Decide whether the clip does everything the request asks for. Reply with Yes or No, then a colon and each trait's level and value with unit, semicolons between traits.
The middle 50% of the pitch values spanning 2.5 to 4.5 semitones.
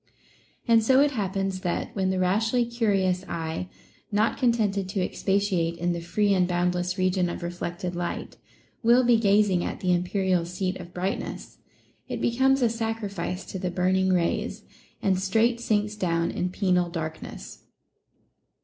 Yes: average, 3.1 semitones